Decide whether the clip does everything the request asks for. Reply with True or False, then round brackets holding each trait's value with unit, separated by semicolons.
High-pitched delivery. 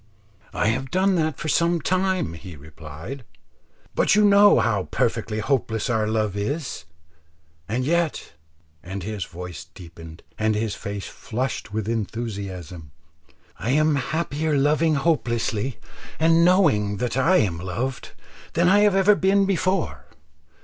False (125 Hz)